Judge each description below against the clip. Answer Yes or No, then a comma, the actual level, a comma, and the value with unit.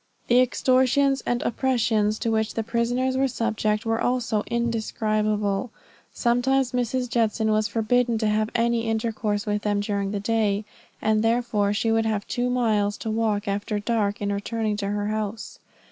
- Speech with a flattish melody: Yes, narrow, 2.1 semitones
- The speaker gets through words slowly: No, average, 160 wpm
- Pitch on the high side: Yes, high, 220 Hz